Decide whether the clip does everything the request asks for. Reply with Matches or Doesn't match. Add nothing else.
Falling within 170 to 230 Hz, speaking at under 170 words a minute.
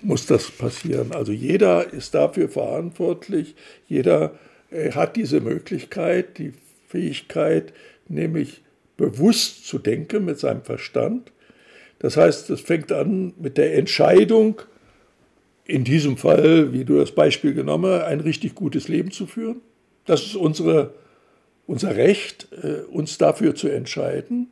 Matches